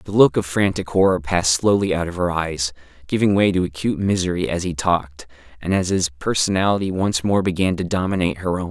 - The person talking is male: Yes, male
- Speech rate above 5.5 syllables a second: Yes, 6.0 syllables/s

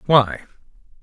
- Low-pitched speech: Yes, low, 125 Hz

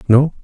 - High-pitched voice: No, low, 130 Hz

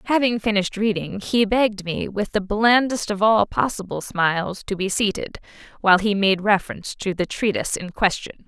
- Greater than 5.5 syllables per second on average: No, 5.4 syllables/s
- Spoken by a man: No, female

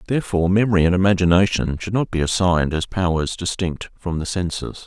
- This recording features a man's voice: Yes, male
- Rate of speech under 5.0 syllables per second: No, 6.0 syllables/s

